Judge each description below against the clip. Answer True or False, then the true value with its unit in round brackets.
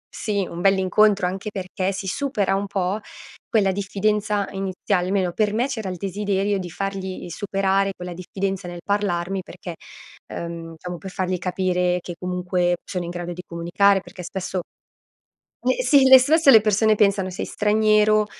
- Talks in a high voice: True (195 Hz)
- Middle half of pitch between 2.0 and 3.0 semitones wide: True (2.4 semitones)